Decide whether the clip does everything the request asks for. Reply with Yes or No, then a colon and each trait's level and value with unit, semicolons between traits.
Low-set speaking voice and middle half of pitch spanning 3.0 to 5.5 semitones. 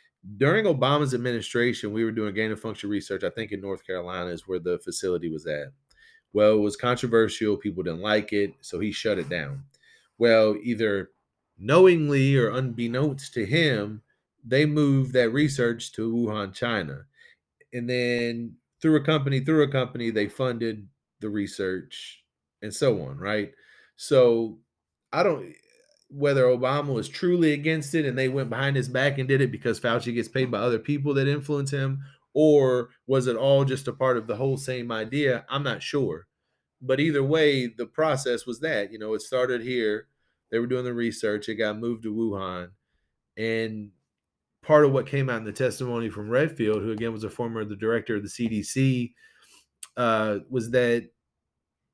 Yes: low, 120 Hz; average, 3.8 semitones